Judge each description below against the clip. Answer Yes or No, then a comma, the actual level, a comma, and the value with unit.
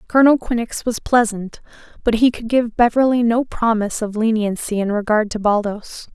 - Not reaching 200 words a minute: Yes, average, 165 wpm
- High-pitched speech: Yes, high, 225 Hz